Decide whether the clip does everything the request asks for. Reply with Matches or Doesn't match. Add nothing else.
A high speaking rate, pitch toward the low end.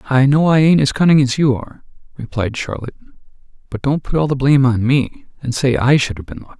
Matches